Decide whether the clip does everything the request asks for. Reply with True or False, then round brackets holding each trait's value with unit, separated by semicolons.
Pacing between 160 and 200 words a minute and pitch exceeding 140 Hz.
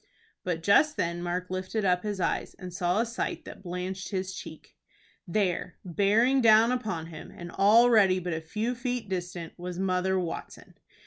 True (170 wpm; 185 Hz)